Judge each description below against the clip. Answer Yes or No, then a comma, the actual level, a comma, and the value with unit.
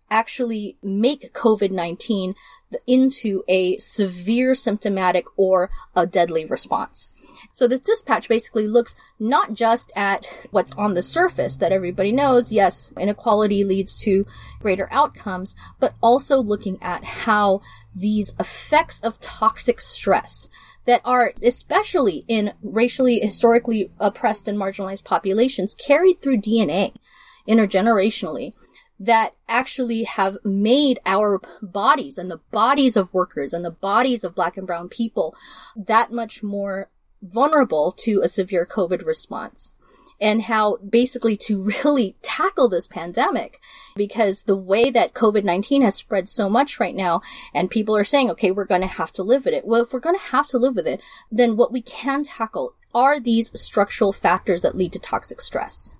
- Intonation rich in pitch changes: No, average, 4.1 semitones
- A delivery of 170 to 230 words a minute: No, average, 150 wpm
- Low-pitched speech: No, high, 215 Hz